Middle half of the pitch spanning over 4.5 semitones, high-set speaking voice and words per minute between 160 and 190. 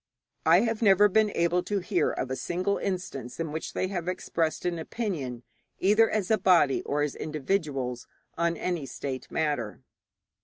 No: average, 5.1 semitones; medium, 170 Hz; average, 165 wpm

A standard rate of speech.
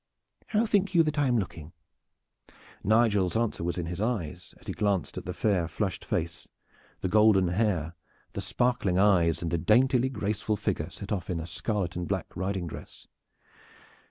Yes: average, 175 wpm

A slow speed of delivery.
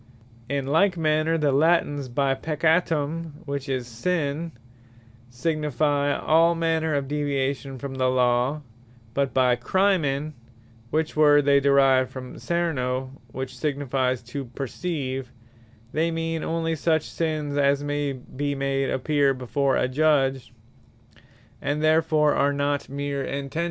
Yes: slow, 125 wpm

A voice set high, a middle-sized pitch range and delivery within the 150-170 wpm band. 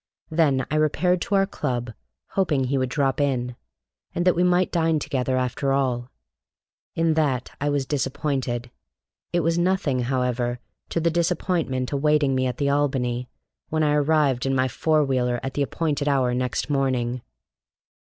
No: medium, 140 Hz; average, 3.7 semitones; average, 160 wpm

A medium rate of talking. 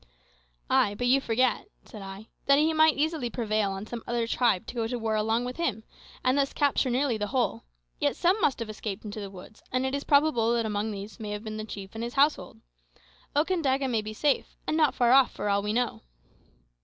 No: fast, 225 wpm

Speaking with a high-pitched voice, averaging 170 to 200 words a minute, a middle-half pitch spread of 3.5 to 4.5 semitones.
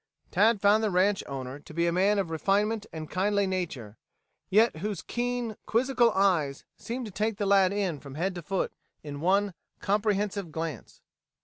Yes: high, 195 Hz; average, 175 wpm; average, 4.1 semitones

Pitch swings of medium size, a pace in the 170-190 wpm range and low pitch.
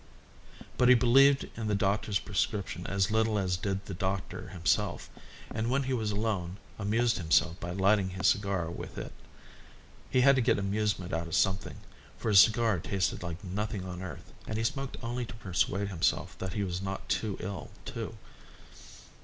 Yes: average, 3.1 semitones; average, 180 wpm; low, 100 Hz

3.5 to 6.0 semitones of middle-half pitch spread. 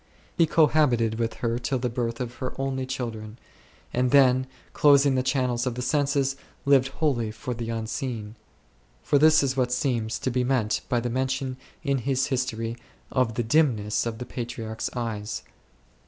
No: narrow, 2.6 semitones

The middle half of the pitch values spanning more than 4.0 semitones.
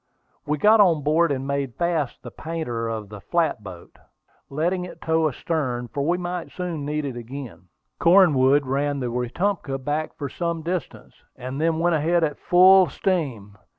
Yes: average, 4.6 semitones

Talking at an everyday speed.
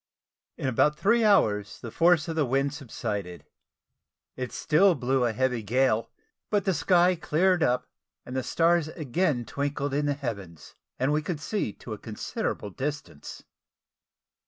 Yes: average, 150 wpm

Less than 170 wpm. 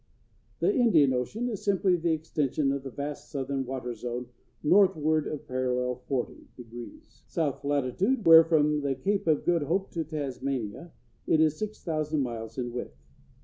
Yes: average, 155 wpm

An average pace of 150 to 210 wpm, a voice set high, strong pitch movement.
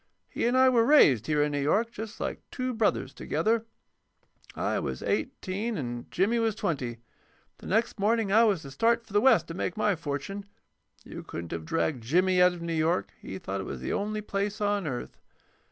Yes: average, 200 wpm; high, 195 Hz; wide, 7.1 semitones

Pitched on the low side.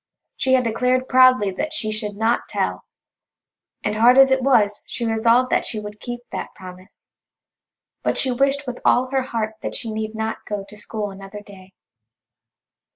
No: high, 225 Hz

